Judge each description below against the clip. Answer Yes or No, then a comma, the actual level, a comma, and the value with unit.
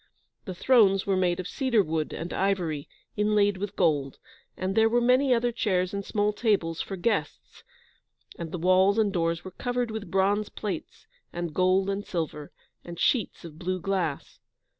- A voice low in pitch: No, high, 190 Hz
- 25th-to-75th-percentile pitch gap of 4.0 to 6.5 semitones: No, average, 3.4 semitones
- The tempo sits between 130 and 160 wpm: No, average, 170 wpm